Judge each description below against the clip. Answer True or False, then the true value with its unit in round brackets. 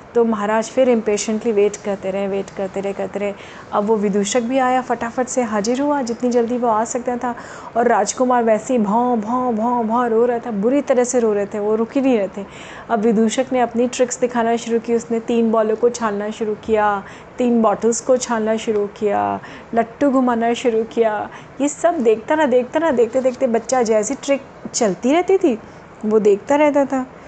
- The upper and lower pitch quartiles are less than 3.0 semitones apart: True (2.6 semitones)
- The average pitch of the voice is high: True (235 Hz)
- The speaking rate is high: True (205 wpm)